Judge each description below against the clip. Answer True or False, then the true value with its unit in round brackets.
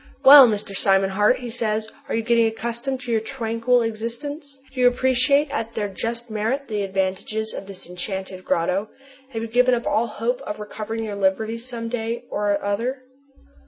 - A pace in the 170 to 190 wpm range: True (180 wpm)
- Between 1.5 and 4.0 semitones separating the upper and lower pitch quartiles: True (2.9 semitones)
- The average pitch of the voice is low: False (225 Hz)